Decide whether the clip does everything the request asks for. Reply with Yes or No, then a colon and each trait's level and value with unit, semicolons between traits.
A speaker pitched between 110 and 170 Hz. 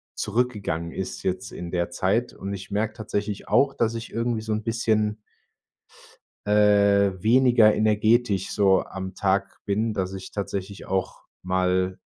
No: low, 100 Hz